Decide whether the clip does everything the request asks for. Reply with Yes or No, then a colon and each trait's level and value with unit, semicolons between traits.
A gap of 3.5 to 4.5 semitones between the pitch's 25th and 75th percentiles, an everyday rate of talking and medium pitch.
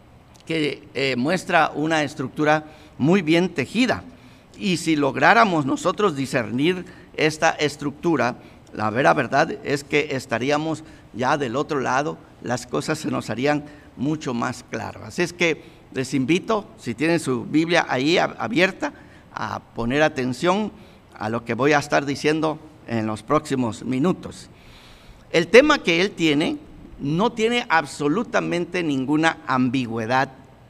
Yes: average, 3.9 semitones; average, 135 wpm; medium, 150 Hz